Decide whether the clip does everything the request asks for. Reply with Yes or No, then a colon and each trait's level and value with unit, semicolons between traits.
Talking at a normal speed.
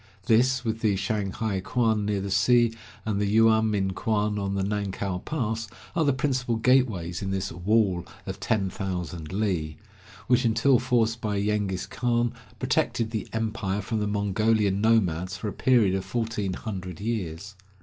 Yes: average, 160 wpm